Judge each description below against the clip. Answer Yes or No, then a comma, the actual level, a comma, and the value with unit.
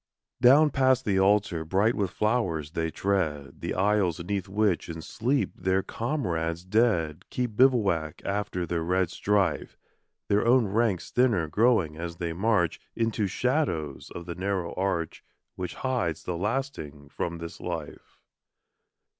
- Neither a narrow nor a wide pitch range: Yes, average, 5.0 semitones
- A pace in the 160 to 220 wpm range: No, average, 145 wpm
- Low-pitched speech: Yes, very low, 95 Hz